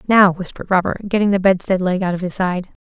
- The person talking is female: Yes, female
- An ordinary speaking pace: No, fast, 230 wpm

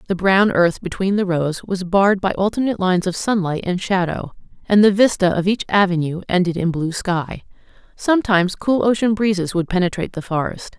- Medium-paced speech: Yes, average, 185 wpm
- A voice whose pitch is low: No, high, 190 Hz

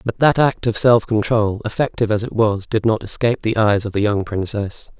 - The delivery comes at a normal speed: No, fast, 230 wpm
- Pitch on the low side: Yes, low, 110 Hz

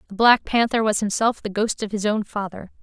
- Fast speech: Yes, fast, 235 wpm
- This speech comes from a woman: Yes, female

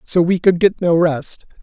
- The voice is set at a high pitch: No, medium, 175 Hz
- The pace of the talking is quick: Yes, fast, 220 wpm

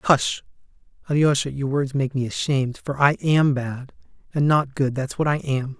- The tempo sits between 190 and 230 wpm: No, average, 175 wpm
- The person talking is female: No, male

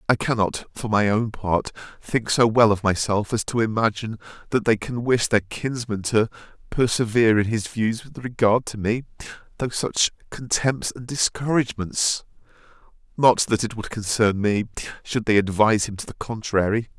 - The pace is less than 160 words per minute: No, average, 165 wpm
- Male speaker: Yes, male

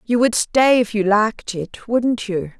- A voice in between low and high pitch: No, high, 220 Hz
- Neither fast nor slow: No, fast, 210 wpm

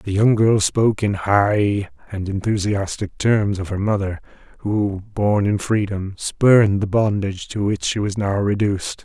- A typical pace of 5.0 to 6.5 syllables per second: No, 4.4 syllables/s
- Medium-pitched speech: No, low, 100 Hz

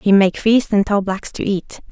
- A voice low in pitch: No, high, 200 Hz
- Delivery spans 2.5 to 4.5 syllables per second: Yes, 4.4 syllables/s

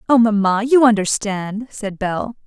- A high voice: Yes, high, 215 Hz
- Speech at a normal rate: Yes, average, 145 wpm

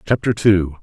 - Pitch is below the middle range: Yes, low, 100 Hz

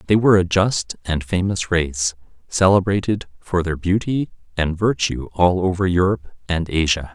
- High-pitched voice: No, very low, 90 Hz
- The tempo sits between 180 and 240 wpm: No, average, 150 wpm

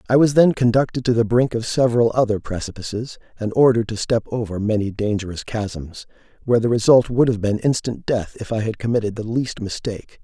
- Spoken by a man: Yes, male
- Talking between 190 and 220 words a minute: Yes, average, 200 wpm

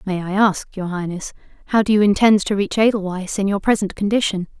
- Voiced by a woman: Yes, female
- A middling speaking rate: No, fast, 210 wpm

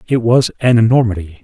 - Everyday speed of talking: Yes, average, 170 wpm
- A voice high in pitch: No, low, 115 Hz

